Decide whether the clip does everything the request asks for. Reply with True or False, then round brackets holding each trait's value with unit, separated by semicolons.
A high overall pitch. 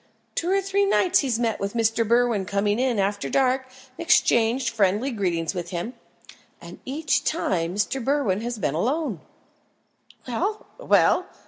True (235 Hz)